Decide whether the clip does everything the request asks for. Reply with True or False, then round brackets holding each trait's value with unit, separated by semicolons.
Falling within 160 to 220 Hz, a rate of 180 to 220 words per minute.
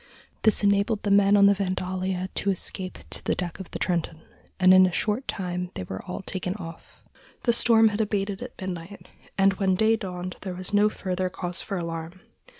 True (190 Hz; 200 wpm)